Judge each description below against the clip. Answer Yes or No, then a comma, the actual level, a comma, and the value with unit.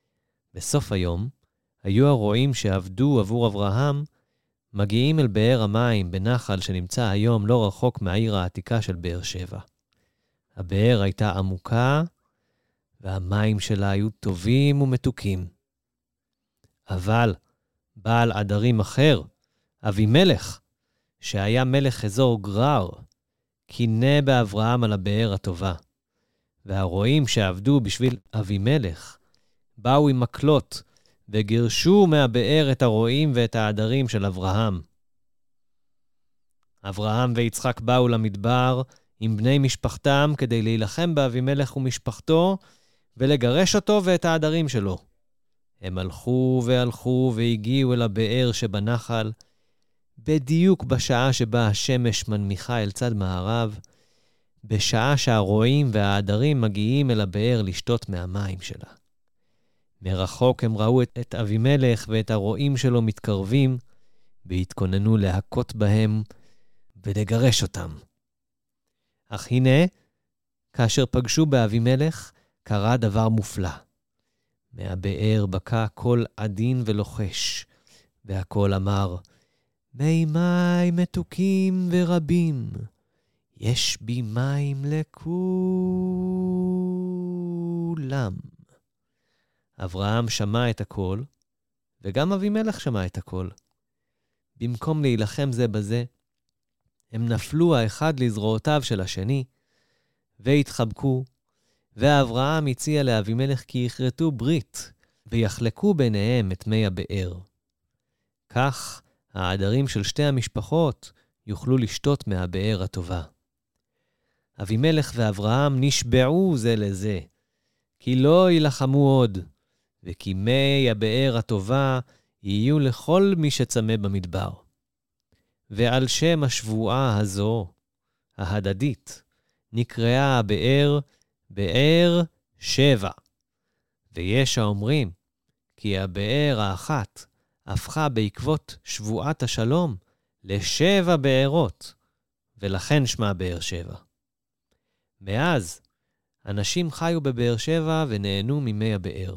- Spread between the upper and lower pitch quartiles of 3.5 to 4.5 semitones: No, average, 4.9 semitones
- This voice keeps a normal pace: No, slow, 90 wpm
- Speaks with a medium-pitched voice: No, low, 115 Hz